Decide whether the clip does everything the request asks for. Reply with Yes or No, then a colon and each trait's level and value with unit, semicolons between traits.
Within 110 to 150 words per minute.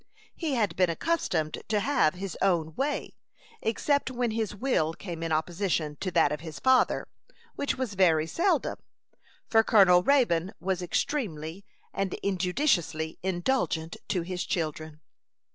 Yes: average, 140 wpm